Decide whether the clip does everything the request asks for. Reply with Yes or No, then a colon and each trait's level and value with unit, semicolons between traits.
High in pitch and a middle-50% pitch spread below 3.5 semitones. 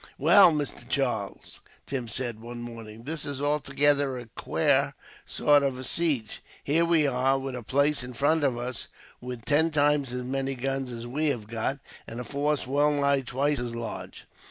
No: low, 135 Hz; average, 3.0 semitones